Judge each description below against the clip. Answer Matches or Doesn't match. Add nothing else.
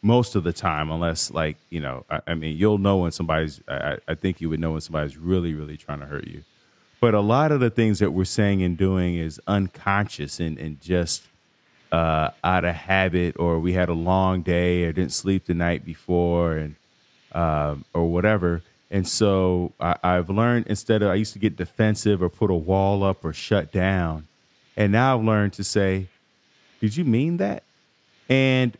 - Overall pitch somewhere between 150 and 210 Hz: Doesn't match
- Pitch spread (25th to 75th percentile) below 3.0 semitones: Doesn't match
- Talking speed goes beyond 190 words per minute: Matches